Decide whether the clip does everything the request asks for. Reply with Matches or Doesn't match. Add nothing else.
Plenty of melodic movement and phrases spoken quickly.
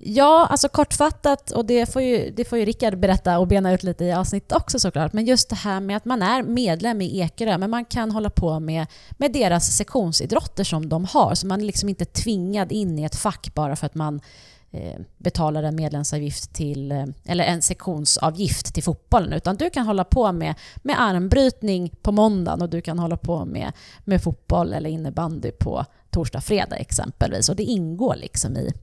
Matches